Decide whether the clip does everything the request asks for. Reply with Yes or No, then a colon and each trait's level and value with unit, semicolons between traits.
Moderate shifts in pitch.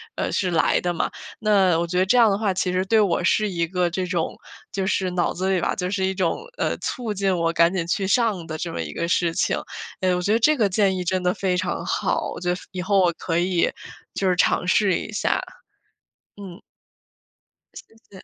No: narrow, 2.1 semitones